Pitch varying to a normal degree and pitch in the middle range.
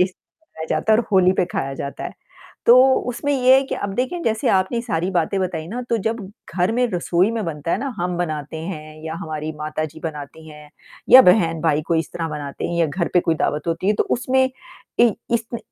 No: wide, 6.3 semitones; medium, 175 Hz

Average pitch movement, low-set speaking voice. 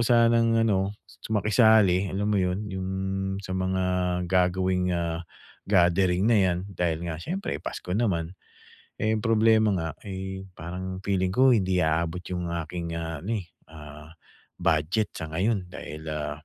Yes: average, 3.3 semitones; very low, 95 Hz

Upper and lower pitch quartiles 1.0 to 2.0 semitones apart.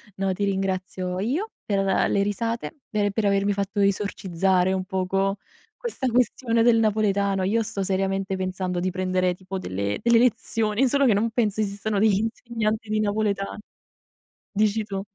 No: narrow, 2.5 semitones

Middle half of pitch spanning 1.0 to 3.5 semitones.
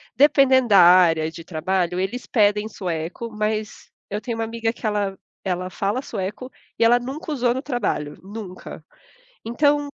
No: average, 4.7 semitones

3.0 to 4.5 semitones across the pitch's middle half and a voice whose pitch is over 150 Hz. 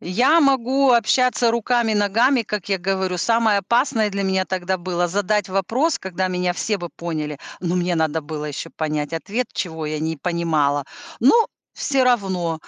No: average, 5.3 semitones; high, 190 Hz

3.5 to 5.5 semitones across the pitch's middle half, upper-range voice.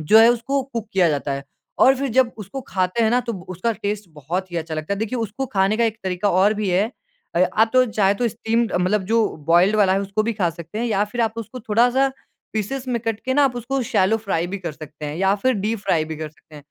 Yes: average, 4.0 semitones; high, 210 Hz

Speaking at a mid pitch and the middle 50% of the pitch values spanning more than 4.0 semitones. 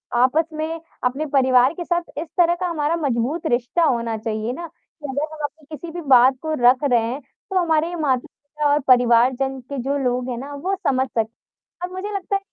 No: very high, 285 Hz; average, 4.6 semitones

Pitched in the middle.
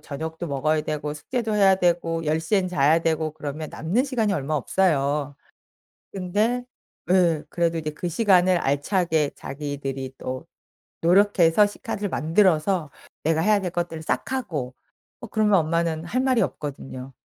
Yes: medium, 165 Hz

